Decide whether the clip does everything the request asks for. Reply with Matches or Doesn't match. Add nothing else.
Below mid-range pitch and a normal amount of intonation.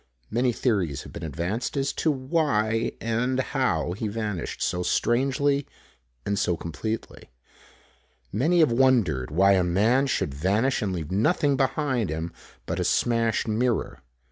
Doesn't match